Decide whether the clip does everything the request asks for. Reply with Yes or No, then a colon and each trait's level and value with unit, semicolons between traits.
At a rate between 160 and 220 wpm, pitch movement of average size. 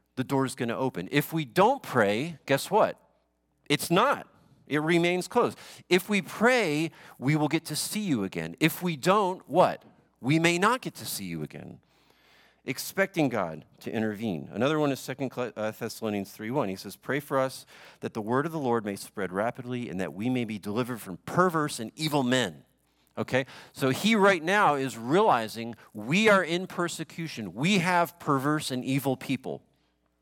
No: average, 180 wpm; wide, 6.3 semitones